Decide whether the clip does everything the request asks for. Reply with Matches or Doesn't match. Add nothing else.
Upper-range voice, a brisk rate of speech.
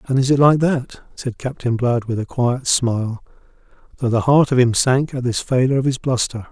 Doesn't match